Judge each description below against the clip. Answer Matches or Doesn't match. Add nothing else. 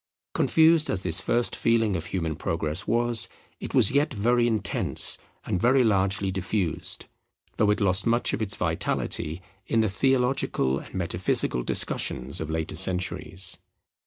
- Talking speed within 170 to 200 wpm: Doesn't match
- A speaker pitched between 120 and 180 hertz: Doesn't match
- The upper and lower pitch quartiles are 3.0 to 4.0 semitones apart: Doesn't match